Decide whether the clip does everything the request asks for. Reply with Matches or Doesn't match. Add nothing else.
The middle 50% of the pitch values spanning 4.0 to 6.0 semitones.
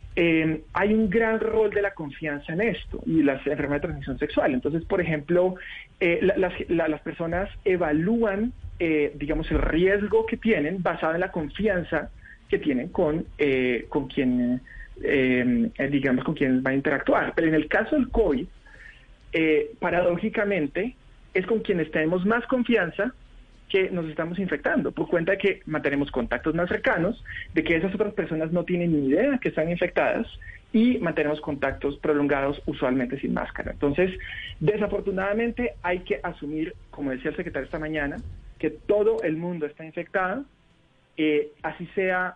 Matches